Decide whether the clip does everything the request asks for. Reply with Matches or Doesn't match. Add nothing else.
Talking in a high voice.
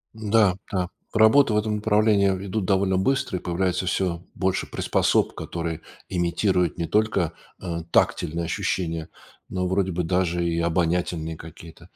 Doesn't match